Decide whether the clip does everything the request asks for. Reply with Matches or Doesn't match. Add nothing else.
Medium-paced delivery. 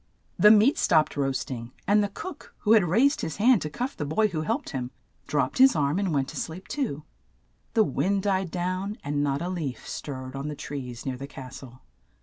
Doesn't match